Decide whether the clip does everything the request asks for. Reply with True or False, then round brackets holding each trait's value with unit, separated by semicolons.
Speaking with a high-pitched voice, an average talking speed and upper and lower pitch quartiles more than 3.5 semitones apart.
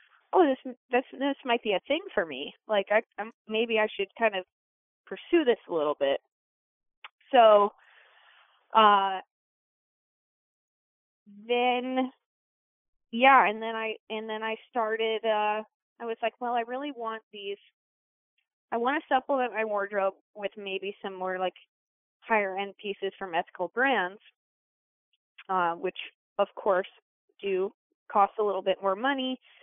True (220 Hz; 145 wpm; 4.4 semitones)